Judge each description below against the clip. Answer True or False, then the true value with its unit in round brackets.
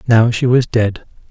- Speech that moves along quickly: False (185 wpm)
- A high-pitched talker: False (115 Hz)